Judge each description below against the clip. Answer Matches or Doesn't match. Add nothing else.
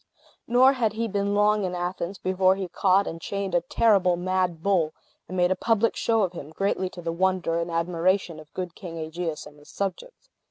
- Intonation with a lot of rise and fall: Doesn't match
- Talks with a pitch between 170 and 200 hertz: Matches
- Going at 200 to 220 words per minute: Matches